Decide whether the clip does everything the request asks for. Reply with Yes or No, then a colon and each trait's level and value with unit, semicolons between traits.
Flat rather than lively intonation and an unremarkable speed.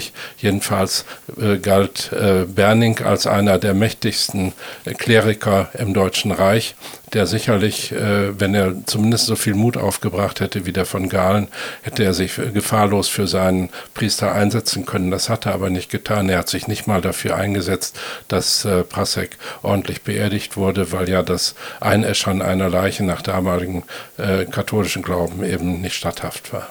Yes: narrow, 2.1 semitones; average, 160 wpm